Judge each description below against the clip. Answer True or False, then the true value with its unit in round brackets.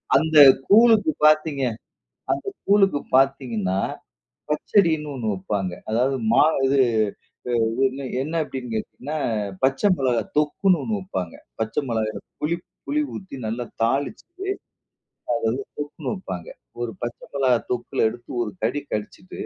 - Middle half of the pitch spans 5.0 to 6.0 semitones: True (5.5 semitones)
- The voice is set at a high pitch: False (135 Hz)